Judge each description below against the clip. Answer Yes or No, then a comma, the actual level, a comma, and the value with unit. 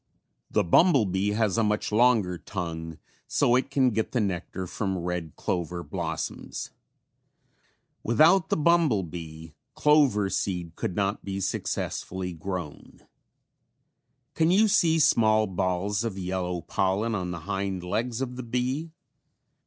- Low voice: Yes, low, 100 Hz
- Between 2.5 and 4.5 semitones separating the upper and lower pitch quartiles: No, wide, 5.5 semitones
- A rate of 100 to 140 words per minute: Yes, slow, 135 wpm